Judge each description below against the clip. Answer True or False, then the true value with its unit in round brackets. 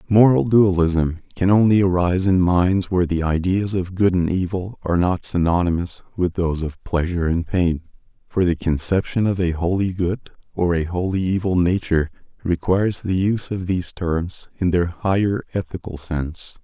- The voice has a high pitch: False (90 Hz)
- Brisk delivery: False (165 wpm)